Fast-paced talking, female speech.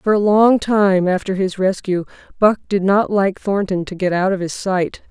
Yes: fast, 210 wpm; female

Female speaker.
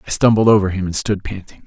No: male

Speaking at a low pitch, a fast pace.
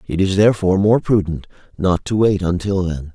No: very low, 95 Hz; average, 190 wpm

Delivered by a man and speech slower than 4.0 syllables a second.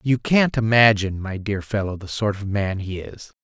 No: male; 4.9 syllables/s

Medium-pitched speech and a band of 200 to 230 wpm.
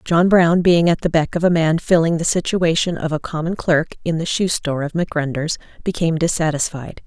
Yes: medium, 165 Hz; fast, 205 wpm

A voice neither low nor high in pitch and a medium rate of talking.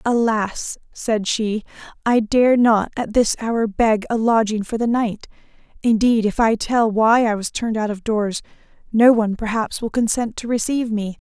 No: high, 225 Hz; average, 180 wpm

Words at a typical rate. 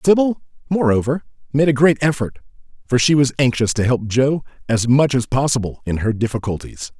Yes: average, 170 wpm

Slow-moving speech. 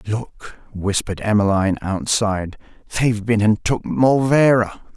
Yes: slow, 110 wpm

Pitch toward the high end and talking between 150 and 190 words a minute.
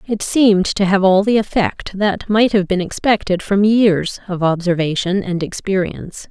Yes: high, 195 Hz; average, 170 wpm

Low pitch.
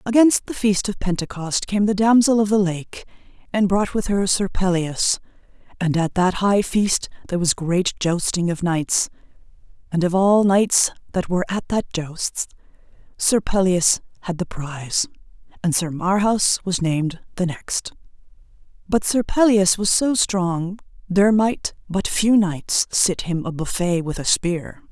No: high, 190 Hz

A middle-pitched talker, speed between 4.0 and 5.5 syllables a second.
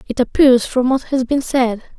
No: very high, 255 Hz; 4.7 syllables/s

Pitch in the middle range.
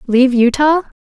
No: very high, 270 Hz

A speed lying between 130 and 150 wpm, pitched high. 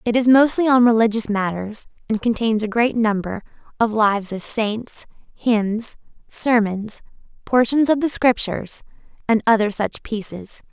Yes: average, 140 wpm; high, 225 Hz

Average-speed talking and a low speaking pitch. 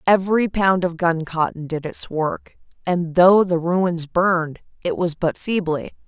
No: average, 160 wpm; medium, 175 Hz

